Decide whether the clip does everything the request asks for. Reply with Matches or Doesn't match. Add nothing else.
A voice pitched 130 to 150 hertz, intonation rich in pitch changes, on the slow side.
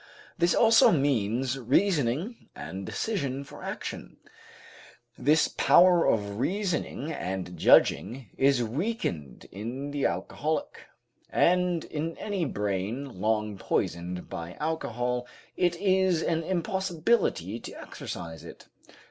Matches